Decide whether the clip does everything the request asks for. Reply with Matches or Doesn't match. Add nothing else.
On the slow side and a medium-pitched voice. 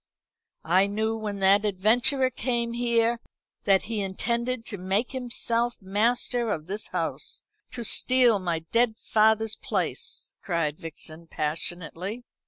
Doesn't match